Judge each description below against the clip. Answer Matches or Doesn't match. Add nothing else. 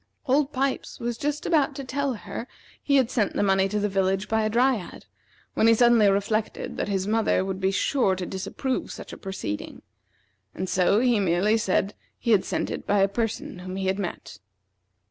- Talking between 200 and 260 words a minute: Matches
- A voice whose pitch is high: Matches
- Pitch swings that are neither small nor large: Matches